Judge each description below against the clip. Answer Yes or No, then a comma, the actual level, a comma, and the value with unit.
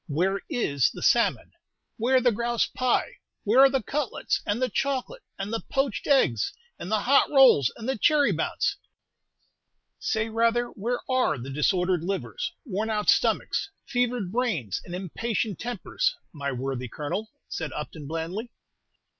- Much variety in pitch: Yes, wide, 6.4 semitones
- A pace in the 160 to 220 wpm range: No, average, 150 wpm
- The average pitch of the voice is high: Yes, high, 220 Hz